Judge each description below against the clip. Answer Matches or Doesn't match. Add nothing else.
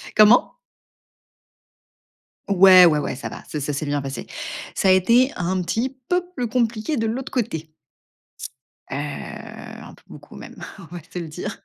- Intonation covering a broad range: Matches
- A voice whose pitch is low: Doesn't match